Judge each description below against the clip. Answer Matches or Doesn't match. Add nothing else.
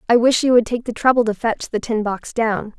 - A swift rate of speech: Matches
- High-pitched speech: Matches